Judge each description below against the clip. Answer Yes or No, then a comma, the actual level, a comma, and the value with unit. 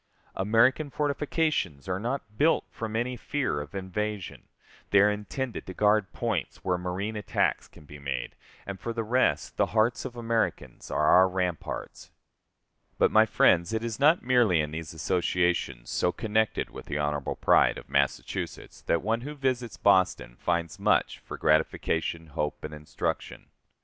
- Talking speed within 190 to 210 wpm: No, average, 160 wpm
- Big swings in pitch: Yes, wide, 5.9 semitones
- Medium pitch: No, low, 100 Hz